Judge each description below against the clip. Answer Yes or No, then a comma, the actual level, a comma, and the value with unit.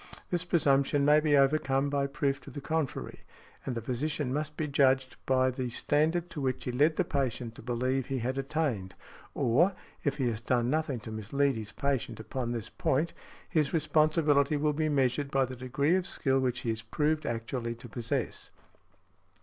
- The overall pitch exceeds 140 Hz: No, low, 135 Hz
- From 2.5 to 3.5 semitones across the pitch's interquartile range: Yes, average, 3.2 semitones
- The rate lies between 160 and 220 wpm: Yes, average, 190 wpm